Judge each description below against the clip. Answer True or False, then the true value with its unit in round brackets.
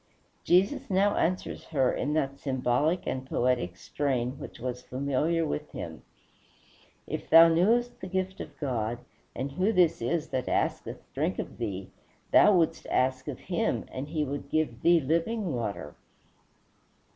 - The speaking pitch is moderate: True (145 Hz)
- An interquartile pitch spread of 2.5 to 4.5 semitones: False (5.2 semitones)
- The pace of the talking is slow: False (150 wpm)